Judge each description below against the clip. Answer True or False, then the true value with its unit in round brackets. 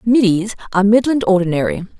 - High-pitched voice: True (205 Hz)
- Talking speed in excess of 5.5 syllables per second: True (6.1 syllables/s)